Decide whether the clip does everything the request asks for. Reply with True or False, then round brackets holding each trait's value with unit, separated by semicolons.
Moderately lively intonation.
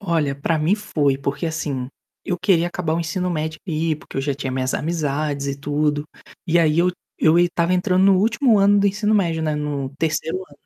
True (3.7 semitones)